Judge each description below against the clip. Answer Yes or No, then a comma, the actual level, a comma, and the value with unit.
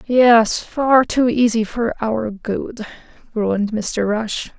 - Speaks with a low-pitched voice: No, high, 225 Hz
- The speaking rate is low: Yes, slow, 130 wpm